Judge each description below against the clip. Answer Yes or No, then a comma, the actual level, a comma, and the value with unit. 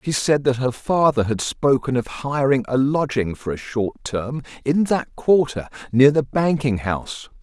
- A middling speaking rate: Yes, average, 180 wpm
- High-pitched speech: No, low, 135 Hz